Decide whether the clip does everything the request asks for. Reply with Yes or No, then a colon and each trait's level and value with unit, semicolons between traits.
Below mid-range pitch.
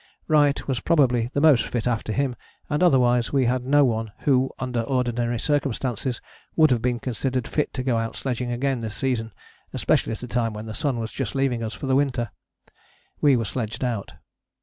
Yes: low, 125 Hz